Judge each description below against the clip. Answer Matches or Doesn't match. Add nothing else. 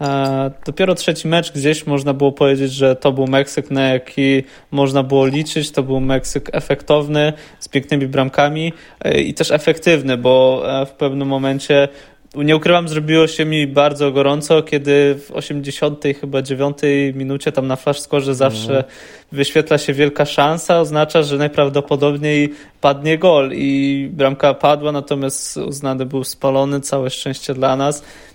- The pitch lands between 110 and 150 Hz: Matches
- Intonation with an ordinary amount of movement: Doesn't match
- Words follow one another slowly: Doesn't match